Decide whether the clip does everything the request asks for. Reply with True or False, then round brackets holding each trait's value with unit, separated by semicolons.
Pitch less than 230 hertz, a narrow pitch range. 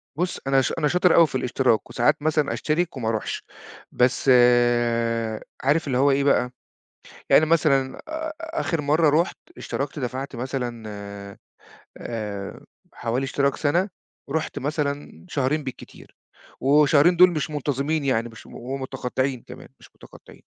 False (140 Hz; 3.3 semitones)